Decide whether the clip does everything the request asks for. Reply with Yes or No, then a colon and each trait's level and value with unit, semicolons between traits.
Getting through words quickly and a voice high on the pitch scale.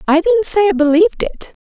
Yes: fast, 220 wpm; very high, 355 Hz